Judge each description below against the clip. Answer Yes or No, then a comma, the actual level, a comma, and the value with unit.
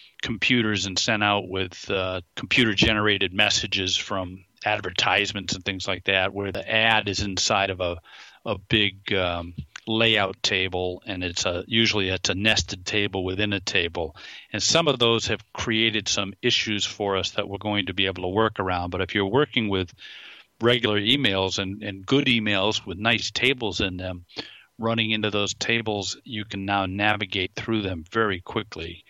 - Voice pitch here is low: Yes, low, 100 Hz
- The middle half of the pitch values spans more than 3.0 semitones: No, average, 2.7 semitones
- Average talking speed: Yes, average, 175 wpm